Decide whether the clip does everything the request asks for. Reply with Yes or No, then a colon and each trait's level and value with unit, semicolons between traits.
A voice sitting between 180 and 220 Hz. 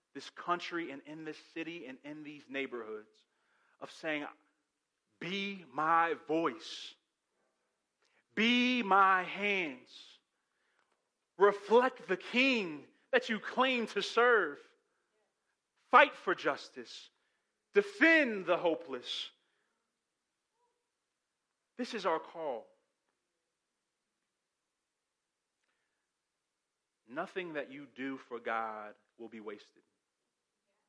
Yes: medium, 185 Hz